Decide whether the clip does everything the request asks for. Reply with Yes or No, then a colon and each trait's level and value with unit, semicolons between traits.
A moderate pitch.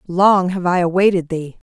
Yes: medium, 180 Hz